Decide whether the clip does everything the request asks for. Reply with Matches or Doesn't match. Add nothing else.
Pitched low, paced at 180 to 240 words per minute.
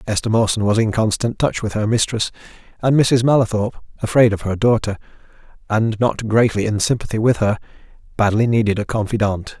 Doesn't match